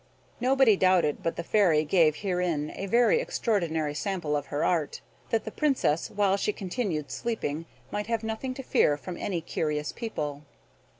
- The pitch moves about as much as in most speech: No, wide, 6.3 semitones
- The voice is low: No, medium, 180 Hz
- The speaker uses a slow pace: No, average, 165 wpm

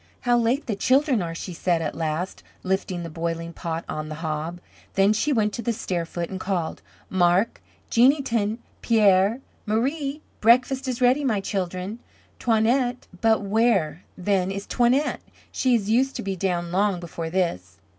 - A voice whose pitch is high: Yes, high, 200 Hz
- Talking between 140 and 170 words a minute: Yes, average, 165 wpm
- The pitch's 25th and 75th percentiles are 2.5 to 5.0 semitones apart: No, wide, 5.5 semitones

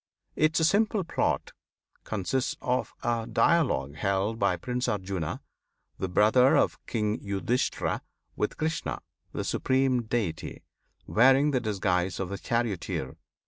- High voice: No, low, 115 Hz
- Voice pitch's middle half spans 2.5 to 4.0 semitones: No, average, 5.1 semitones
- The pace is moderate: No, slow, 120 wpm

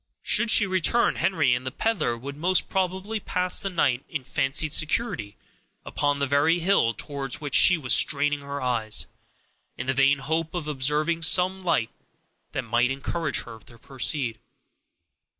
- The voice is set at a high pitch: No, medium, 145 Hz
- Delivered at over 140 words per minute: Yes, average, 160 wpm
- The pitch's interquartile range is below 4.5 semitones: No, average, 5.2 semitones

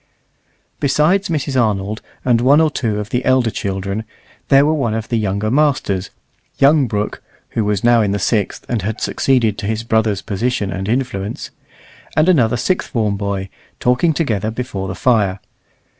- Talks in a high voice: No, low, 115 Hz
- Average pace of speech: Yes, average, 170 wpm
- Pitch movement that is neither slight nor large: Yes, average, 4.3 semitones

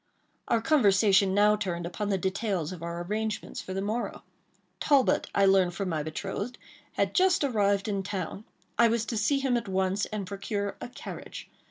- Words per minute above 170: Yes, average, 180 wpm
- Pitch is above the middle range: Yes, high, 200 Hz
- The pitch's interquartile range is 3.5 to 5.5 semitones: No, average, 2.7 semitones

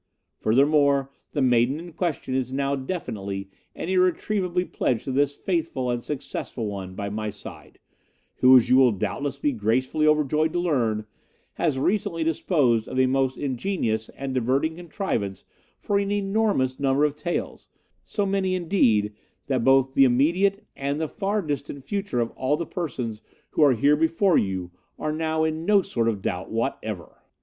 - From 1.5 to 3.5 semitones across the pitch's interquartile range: No, wide, 5.5 semitones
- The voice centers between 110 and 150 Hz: Yes, medium, 140 Hz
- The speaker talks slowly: No, average, 165 wpm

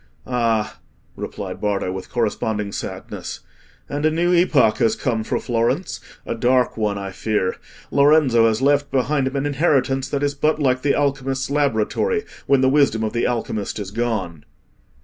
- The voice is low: Yes, low, 130 Hz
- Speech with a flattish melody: No, average, 4.4 semitones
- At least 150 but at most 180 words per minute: Yes, average, 160 wpm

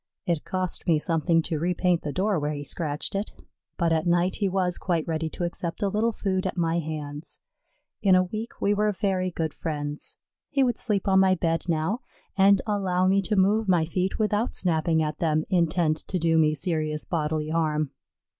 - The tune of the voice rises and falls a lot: No, average, 3.3 semitones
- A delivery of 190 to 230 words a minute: Yes, average, 195 wpm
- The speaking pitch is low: No, medium, 175 Hz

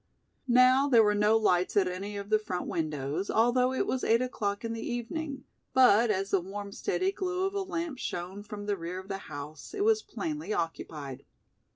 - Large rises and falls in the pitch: Yes, wide, 5.7 semitones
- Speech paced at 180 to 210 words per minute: Yes, average, 200 wpm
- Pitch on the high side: Yes, high, 215 Hz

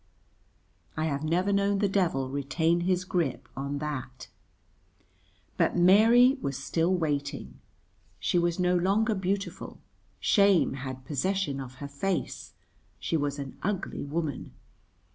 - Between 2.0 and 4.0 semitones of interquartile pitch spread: No, average, 5.3 semitones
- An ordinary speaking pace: No, slow, 125 wpm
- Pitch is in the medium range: Yes, medium, 165 Hz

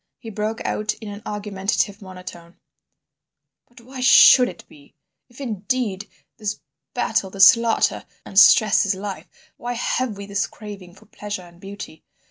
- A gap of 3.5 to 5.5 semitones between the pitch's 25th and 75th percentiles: No, average, 2.7 semitones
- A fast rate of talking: No, average, 150 wpm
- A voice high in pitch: Yes, high, 205 Hz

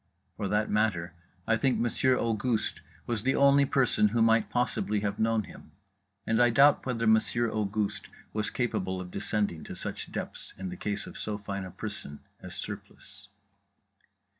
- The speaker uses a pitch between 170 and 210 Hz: No, low, 110 Hz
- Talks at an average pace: Yes, average, 165 wpm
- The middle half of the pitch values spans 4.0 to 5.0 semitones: No, average, 2.7 semitones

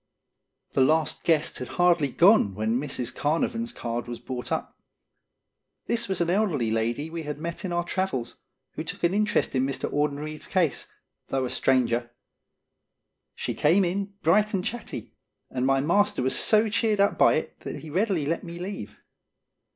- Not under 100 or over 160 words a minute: No, average, 170 wpm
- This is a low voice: No, medium, 160 Hz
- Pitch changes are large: Yes, wide, 6.6 semitones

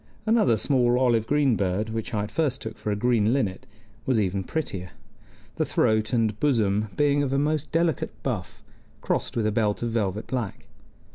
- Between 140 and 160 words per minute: No, average, 185 wpm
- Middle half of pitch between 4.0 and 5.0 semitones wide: Yes, average, 4.5 semitones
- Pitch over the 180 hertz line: No, low, 115 Hz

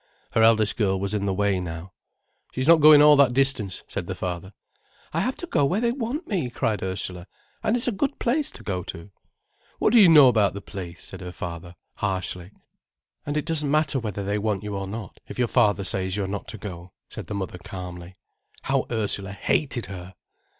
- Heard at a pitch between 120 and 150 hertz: No, low, 105 Hz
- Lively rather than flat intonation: Yes, wide, 7.1 semitones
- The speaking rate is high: Yes, fast, 215 wpm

